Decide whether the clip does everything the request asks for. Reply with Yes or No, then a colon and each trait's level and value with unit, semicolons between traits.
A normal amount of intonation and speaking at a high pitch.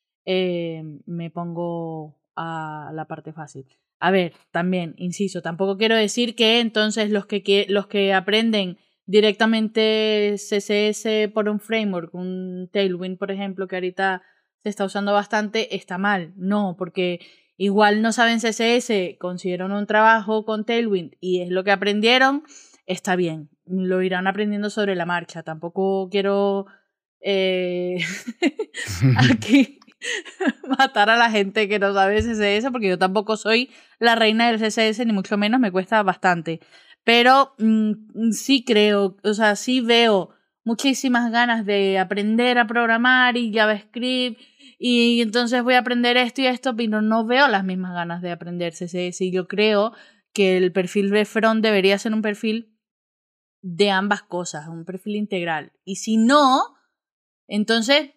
Yes: average, 3.5 semitones; high, 205 Hz